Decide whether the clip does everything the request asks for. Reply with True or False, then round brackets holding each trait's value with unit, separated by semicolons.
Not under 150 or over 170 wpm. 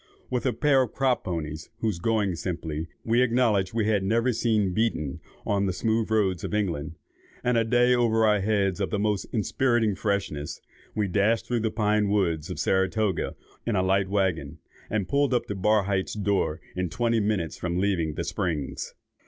False (180 wpm)